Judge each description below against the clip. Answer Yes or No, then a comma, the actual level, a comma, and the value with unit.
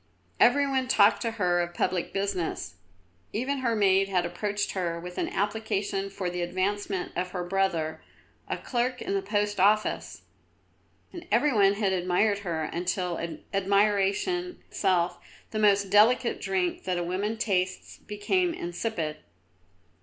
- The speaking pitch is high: Yes, high, 195 Hz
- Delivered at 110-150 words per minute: Yes, average, 145 wpm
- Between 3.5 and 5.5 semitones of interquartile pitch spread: No, average, 3.0 semitones